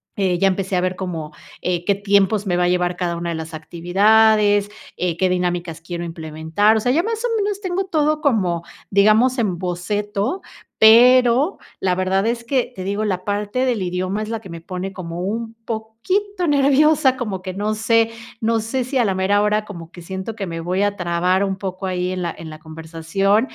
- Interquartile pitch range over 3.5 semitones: Yes, average, 4.1 semitones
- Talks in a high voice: Yes, high, 195 Hz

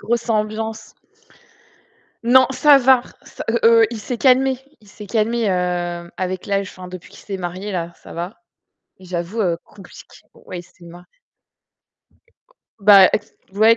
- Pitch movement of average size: Yes, average, 4.2 semitones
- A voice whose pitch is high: Yes, high, 200 Hz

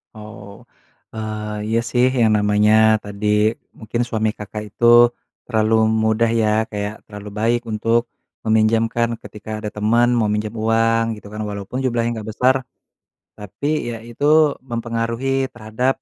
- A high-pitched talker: No, low, 110 Hz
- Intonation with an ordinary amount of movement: No, narrow, 1.7 semitones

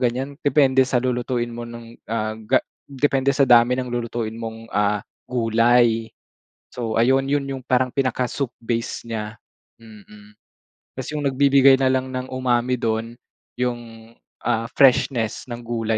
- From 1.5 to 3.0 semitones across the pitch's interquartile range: Yes, narrow, 2.4 semitones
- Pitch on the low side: Yes, low, 120 Hz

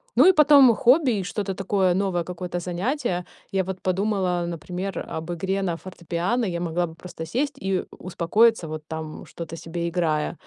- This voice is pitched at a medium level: Yes, medium, 180 Hz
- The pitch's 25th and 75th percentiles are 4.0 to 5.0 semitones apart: No, average, 2.8 semitones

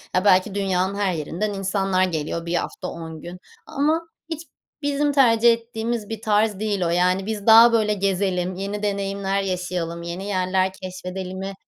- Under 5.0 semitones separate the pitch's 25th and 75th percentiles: Yes, average, 2.9 semitones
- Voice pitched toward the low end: No, high, 195 Hz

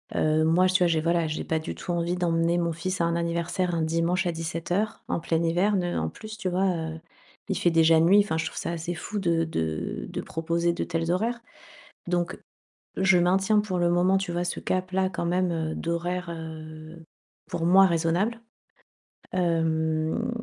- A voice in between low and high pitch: Yes, medium, 170 Hz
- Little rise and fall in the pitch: Yes, narrow, 1.9 semitones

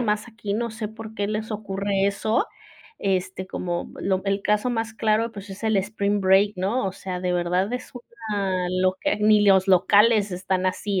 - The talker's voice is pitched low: No, high, 200 Hz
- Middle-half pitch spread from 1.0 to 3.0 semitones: Yes, narrow, 2.5 semitones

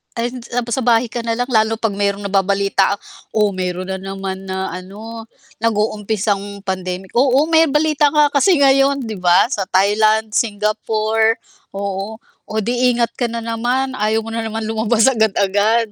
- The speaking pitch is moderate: No, high, 220 Hz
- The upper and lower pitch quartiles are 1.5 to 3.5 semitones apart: Yes, average, 2.9 semitones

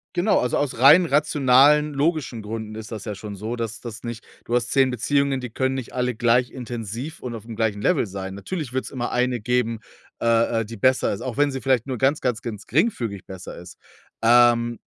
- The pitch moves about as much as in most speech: Yes, average, 3.0 semitones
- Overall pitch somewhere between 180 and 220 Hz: No, low, 120 Hz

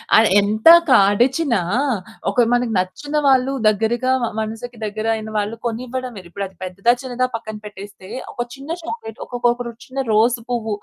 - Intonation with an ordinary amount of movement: Yes, average, 3.1 semitones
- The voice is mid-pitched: No, high, 230 Hz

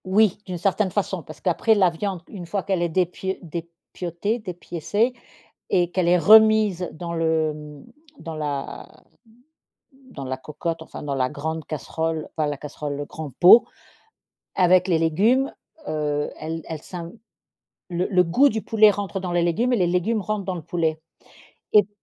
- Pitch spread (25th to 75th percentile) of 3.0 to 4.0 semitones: Yes, average, 3.7 semitones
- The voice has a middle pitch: Yes, medium, 175 Hz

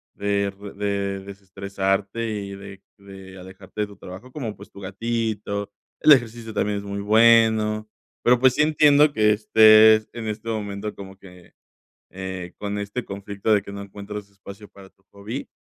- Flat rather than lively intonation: Yes, narrow, 2.0 semitones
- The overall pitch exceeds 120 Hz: No, low, 100 Hz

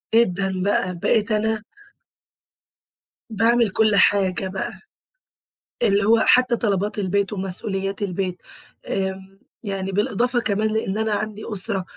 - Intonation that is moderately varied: No, narrow, 2.3 semitones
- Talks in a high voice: Yes, high, 200 Hz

